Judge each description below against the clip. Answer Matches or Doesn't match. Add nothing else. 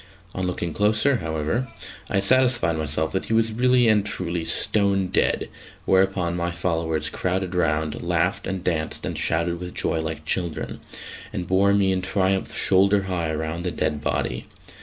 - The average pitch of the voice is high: Doesn't match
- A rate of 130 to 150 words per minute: Doesn't match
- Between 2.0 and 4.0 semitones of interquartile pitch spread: Matches